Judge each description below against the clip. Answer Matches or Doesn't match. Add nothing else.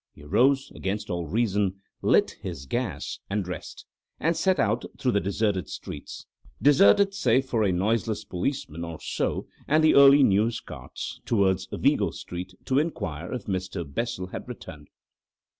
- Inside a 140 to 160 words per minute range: Matches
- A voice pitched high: Doesn't match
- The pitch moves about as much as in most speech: Doesn't match